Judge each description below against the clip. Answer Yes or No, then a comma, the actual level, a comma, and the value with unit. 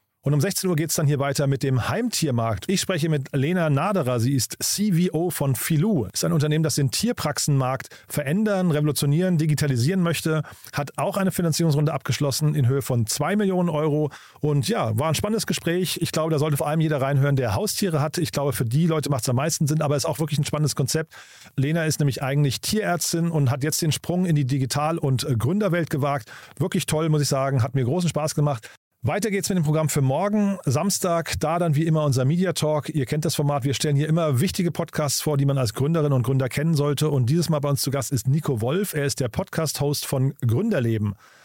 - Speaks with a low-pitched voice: No, medium, 150 Hz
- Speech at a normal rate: No, fast, 225 wpm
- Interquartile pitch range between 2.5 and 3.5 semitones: Yes, average, 3.2 semitones